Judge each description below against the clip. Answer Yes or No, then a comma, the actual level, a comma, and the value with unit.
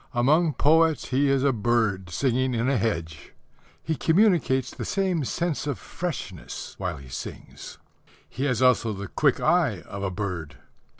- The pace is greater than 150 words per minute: Yes, average, 160 wpm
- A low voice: Yes, low, 125 Hz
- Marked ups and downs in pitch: Yes, wide, 6.9 semitones